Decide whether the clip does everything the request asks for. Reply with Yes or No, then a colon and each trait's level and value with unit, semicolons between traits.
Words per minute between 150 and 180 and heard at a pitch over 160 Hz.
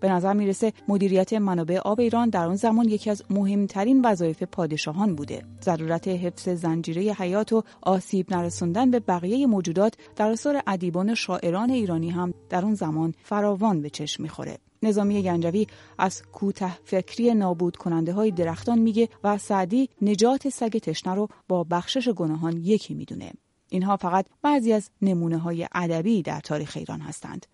Yes: fast, 155 wpm; high, 190 Hz